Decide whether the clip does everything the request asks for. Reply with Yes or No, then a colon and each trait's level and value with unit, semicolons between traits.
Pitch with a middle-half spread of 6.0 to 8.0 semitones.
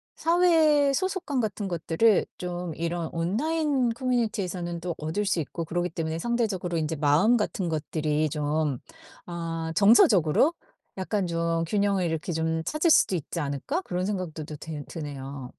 No: wide, 5.5 semitones